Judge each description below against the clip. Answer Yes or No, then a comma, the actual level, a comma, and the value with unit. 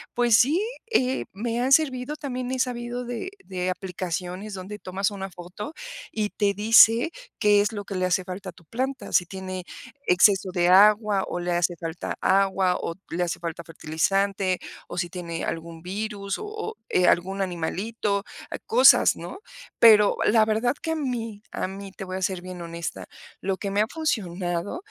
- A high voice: Yes, high, 195 Hz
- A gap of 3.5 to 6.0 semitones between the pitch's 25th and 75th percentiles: Yes, average, 4.1 semitones